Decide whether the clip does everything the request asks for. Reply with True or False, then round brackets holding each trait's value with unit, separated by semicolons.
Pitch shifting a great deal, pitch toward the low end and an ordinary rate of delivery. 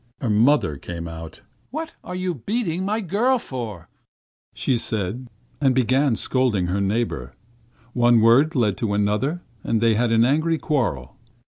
True (6.5 semitones; 120 Hz; 150 wpm)